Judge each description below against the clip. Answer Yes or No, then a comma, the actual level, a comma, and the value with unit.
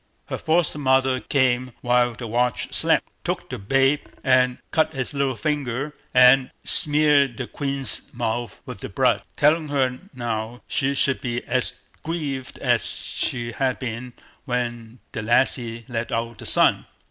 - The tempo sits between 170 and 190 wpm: No, average, 150 wpm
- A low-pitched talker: Yes, low, 125 Hz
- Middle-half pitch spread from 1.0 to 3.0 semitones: Yes, narrow, 2.5 semitones